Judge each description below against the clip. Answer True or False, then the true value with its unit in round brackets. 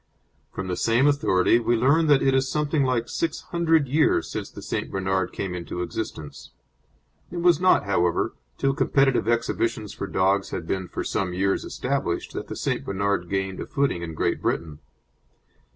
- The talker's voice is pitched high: False (110 Hz)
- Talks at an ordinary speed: True (175 wpm)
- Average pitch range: False (6.9 semitones)